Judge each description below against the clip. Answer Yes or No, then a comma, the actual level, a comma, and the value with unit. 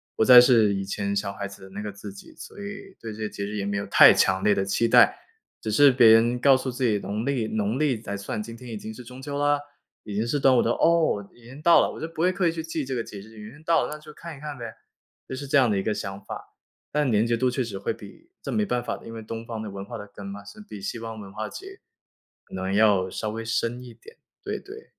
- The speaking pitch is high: No, low, 115 Hz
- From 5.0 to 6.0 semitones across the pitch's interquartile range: Yes, average, 5.3 semitones